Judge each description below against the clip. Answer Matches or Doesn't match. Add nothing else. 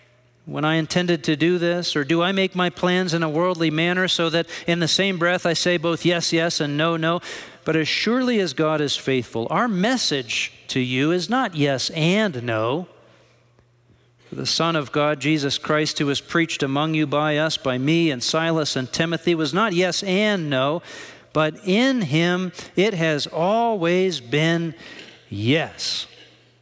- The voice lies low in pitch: Doesn't match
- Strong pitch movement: Doesn't match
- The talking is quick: Doesn't match